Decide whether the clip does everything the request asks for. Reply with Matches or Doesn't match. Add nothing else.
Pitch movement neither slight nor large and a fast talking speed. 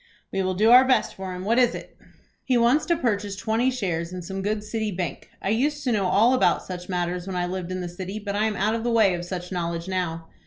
Matches